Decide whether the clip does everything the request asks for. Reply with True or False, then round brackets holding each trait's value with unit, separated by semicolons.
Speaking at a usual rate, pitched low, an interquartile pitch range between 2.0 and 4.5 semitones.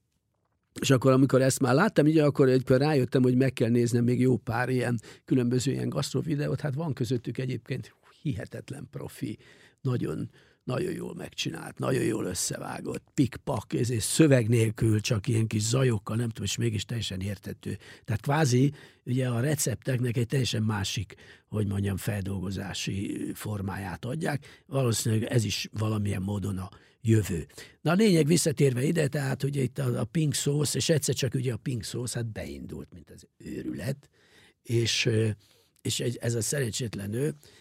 True (155 wpm; 125 Hz; 4.0 semitones)